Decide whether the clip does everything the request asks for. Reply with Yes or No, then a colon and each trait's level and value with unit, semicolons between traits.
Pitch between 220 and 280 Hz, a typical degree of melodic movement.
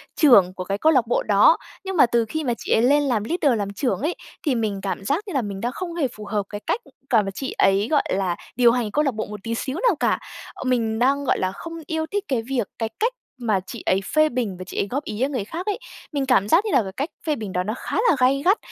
No: high, 245 Hz; wide, 6.1 semitones